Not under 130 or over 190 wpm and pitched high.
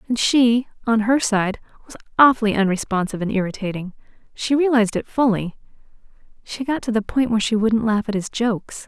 Yes: average, 160 wpm; high, 220 Hz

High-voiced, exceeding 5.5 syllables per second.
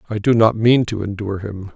No: low, 105 Hz; 5.8 syllables/s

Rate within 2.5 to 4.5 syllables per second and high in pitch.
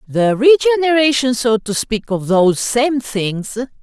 Yes: 4.1 syllables/s; high, 245 Hz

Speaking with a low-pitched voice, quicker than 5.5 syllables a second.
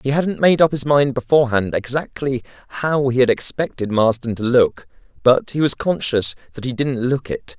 No: low, 130 Hz; 5.0 syllables/s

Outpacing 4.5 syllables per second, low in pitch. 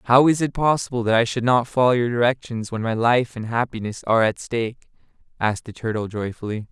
Yes: 6.0 syllables/s; low, 120 Hz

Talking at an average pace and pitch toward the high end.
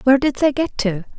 No: fast, 255 wpm; very high, 255 Hz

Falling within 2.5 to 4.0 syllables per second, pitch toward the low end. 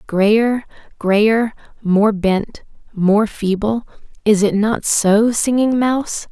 No: 3.1 syllables/s; high, 215 Hz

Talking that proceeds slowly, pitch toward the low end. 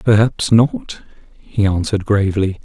Yes: slow, 115 wpm; low, 100 Hz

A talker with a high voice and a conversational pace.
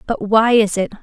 No: high, 215 Hz; fast, 235 wpm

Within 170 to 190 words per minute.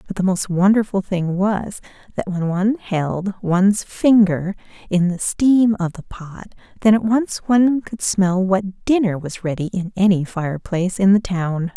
Yes: average, 180 wpm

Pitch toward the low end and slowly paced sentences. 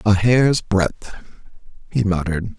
Yes: low, 105 Hz; slow, 115 wpm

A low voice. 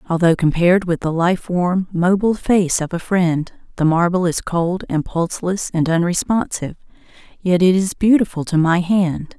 No: medium, 175 Hz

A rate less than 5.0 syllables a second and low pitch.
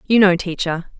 No: 4.8 syllables/s; medium, 185 Hz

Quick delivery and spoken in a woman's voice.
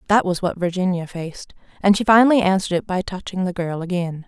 Yes: fast, 210 wpm; female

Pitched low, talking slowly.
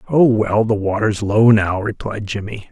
No: low, 105 Hz; average, 175 wpm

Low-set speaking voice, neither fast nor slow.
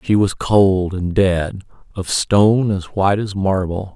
Yes: very low, 95 Hz; average, 150 wpm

